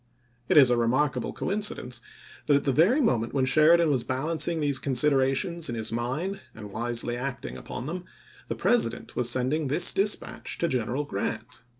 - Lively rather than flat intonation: No, average, 4.8 semitones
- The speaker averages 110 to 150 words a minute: No, average, 180 wpm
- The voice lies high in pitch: No, low, 135 Hz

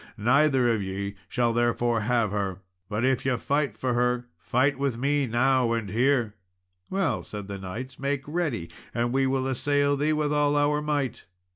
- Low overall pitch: Yes, low, 125 Hz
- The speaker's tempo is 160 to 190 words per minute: Yes, average, 180 wpm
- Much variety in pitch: No, average, 3.8 semitones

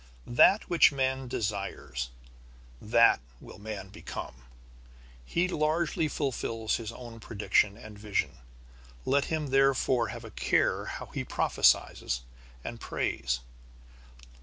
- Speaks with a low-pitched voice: Yes, low, 115 Hz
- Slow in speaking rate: Yes, slow, 110 wpm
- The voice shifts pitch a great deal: No, average, 4.9 semitones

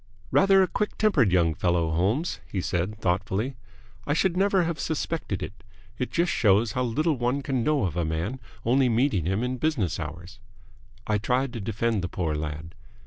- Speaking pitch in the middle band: No, low, 115 Hz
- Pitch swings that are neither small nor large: No, wide, 7.7 semitones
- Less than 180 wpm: No, average, 185 wpm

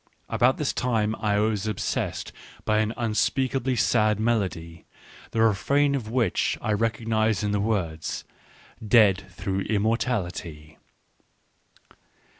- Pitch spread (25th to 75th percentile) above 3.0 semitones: No, narrow, 2.5 semitones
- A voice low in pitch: Yes, low, 110 Hz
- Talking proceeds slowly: Yes, slow, 130 wpm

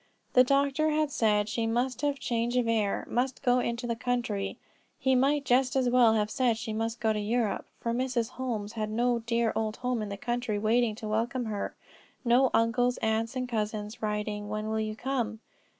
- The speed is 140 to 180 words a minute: No, average, 200 wpm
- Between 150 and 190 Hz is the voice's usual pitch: No, high, 235 Hz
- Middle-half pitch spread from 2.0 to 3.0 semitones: Yes, narrow, 2.5 semitones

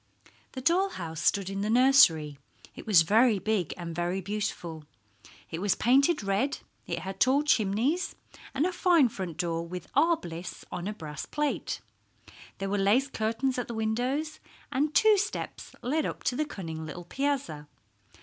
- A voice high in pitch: Yes, high, 215 Hz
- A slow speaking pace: No, average, 170 wpm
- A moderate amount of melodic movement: No, wide, 7.7 semitones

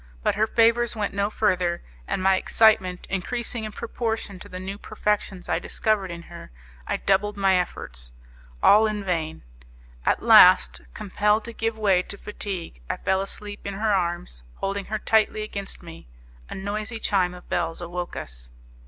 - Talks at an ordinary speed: Yes, average, 170 wpm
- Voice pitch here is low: No, high, 195 Hz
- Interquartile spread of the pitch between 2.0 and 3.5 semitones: Yes, average, 3.1 semitones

